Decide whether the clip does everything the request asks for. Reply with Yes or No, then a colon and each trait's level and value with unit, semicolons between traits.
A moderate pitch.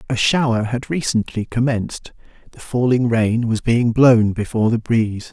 No: low, 115 Hz